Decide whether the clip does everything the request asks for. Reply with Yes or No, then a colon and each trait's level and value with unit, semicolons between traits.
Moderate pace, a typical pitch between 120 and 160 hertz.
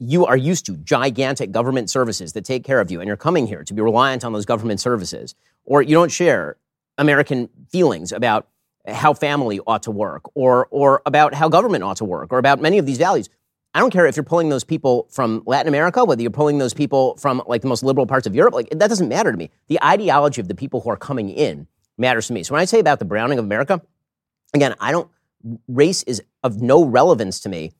No: fast, 235 wpm; low, 135 Hz